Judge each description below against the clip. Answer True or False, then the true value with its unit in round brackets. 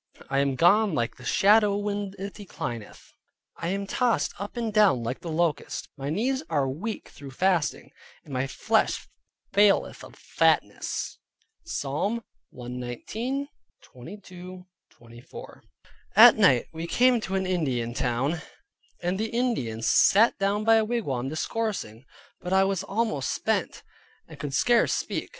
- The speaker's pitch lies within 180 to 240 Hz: True (185 Hz)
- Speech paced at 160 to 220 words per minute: False (140 wpm)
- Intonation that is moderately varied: False (7.8 semitones)